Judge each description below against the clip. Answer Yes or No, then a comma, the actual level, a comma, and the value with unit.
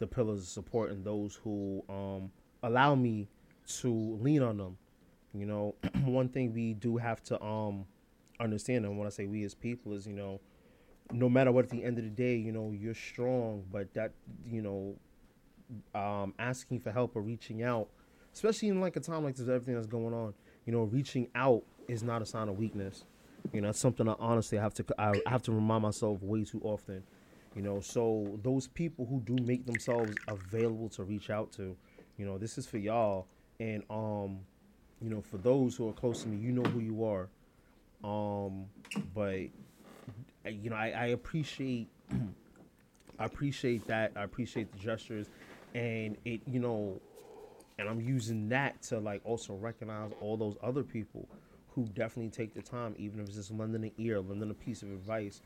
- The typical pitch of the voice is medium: No, low, 110 Hz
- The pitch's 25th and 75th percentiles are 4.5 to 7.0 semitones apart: No, average, 2.8 semitones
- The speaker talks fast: No, average, 195 wpm